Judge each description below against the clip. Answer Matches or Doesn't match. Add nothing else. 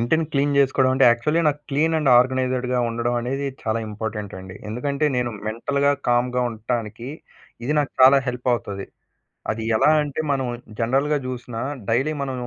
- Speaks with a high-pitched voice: Doesn't match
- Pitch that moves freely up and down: Doesn't match